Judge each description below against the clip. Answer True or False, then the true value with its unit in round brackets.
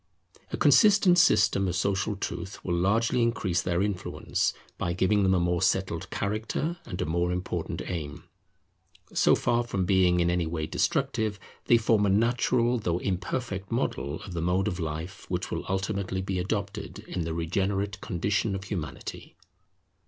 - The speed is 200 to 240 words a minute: False (160 wpm)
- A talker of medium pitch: False (95 Hz)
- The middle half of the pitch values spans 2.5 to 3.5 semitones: True (3.1 semitones)